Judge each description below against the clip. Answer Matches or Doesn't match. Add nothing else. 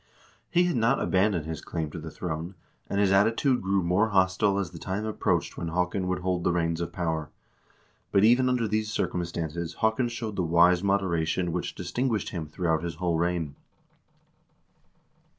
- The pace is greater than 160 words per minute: Matches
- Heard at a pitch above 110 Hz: Doesn't match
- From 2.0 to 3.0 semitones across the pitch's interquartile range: Doesn't match